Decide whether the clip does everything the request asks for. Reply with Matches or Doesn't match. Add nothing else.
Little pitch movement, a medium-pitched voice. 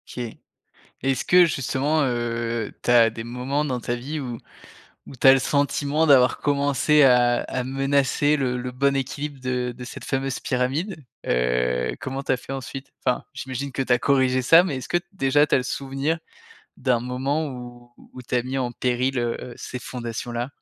Doesn't match